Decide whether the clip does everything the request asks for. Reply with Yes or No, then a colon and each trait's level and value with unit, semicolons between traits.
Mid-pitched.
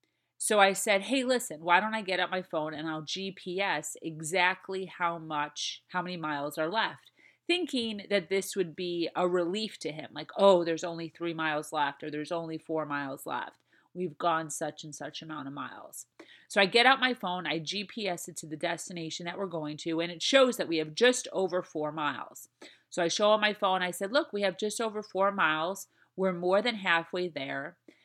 Yes: medium, 180 Hz